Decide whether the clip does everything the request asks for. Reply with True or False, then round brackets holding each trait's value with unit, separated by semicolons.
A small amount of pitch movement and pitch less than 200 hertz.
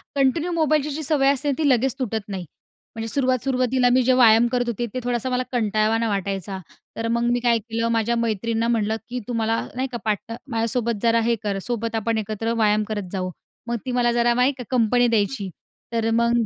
False (2.3 semitones; 235 Hz)